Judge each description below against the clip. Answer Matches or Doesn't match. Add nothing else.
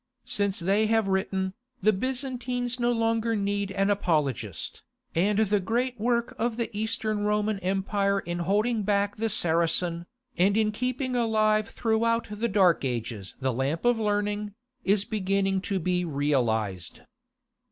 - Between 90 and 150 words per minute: Matches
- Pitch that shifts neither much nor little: Matches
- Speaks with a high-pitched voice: Matches